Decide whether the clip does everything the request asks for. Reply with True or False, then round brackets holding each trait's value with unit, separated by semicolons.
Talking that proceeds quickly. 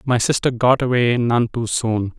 False (190 wpm)